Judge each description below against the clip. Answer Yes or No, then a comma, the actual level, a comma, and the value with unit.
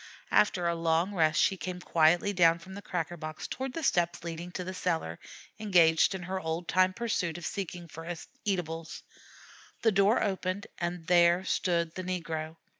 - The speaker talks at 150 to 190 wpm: Yes, average, 175 wpm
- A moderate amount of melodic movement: No, narrow, 2.2 semitones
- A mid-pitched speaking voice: Yes, medium, 175 Hz